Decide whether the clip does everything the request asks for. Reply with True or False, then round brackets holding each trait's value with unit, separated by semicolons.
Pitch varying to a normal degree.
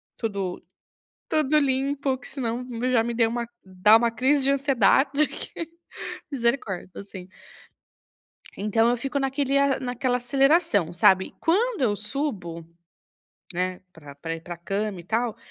False (5.7 semitones)